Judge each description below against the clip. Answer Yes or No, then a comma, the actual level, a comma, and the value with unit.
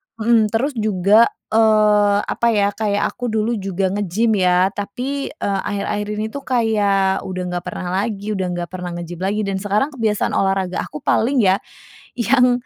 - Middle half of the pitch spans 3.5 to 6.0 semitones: No, average, 2.7 semitones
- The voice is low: No, high, 205 Hz